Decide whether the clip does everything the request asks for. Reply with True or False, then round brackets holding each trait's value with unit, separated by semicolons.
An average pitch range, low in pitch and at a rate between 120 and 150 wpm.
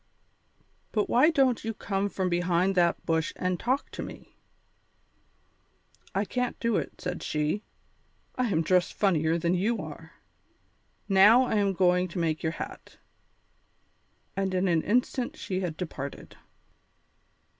False (3.9 semitones; 185 Hz; 140 wpm)